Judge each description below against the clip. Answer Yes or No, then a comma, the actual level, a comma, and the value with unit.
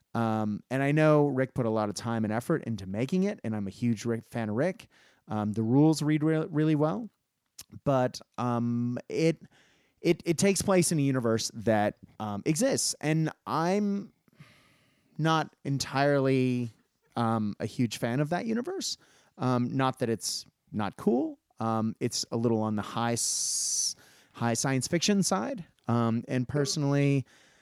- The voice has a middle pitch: No, low, 130 Hz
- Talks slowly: No, average, 165 wpm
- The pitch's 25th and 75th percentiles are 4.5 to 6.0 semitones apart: Yes, wide, 5.4 semitones